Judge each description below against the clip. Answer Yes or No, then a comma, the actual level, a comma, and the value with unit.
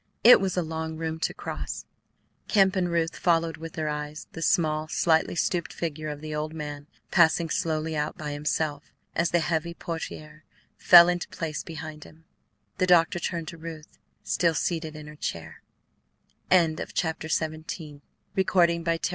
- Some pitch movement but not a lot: No, narrow, 1.7 semitones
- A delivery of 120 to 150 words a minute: No, average, 165 wpm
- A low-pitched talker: No, medium, 160 Hz